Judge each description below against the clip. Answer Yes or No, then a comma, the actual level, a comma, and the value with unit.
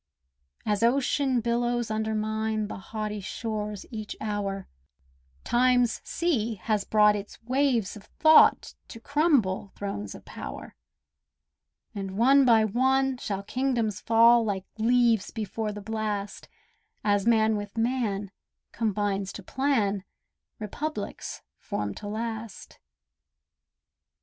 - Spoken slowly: Yes, slow, 110 wpm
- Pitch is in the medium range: No, high, 220 Hz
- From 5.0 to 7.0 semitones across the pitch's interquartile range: No, average, 2.7 semitones